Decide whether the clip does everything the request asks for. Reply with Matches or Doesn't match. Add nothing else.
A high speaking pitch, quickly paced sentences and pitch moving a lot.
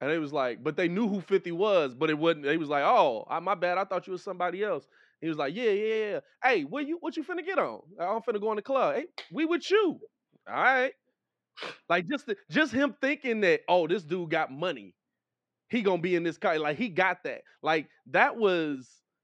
Matches